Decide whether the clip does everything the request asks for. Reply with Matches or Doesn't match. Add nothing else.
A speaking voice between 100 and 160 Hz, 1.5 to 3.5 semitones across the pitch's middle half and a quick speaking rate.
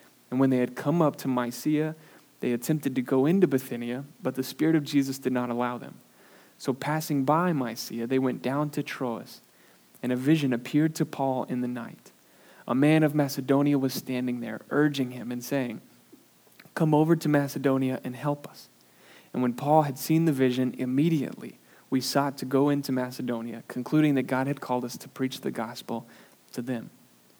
Doesn't match